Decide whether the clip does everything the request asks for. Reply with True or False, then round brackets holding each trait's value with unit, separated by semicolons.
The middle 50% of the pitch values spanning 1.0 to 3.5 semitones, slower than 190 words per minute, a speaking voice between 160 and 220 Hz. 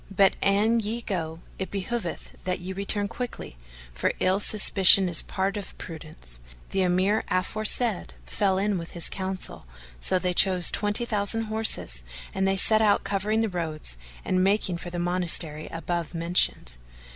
True (2.9 semitones; 155 wpm; 190 Hz)